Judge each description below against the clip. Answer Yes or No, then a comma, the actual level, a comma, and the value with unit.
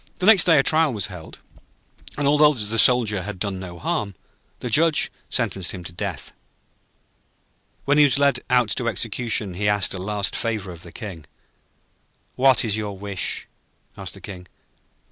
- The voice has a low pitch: Yes, low, 105 Hz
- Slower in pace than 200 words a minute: Yes, average, 165 wpm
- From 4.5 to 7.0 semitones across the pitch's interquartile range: Yes, average, 5.2 semitones